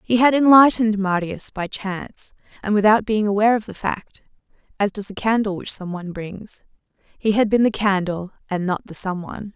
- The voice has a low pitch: No, high, 205 Hz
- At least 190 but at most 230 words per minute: Yes, average, 195 wpm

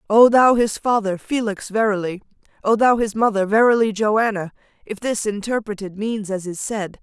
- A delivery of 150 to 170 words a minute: Yes, average, 160 wpm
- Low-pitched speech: No, high, 215 Hz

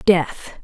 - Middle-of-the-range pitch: Yes, medium, 170 Hz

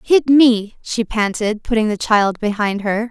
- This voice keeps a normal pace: Yes, average, 175 wpm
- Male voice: No, female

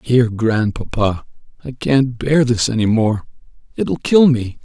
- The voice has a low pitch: Yes, low, 120 Hz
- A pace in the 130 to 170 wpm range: Yes, average, 140 wpm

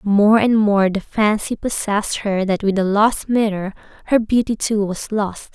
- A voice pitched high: Yes, high, 210 Hz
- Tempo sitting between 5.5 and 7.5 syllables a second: No, 4.4 syllables/s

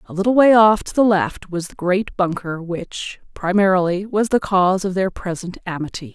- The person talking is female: Yes, female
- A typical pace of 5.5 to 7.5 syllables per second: No, 5.0 syllables/s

